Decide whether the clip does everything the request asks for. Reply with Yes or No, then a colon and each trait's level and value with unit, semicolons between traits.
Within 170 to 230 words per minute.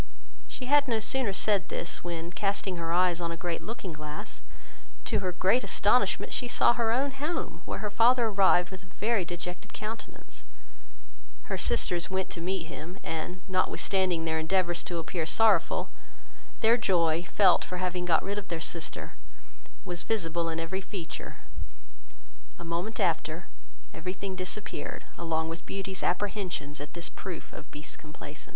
No: average, 160 wpm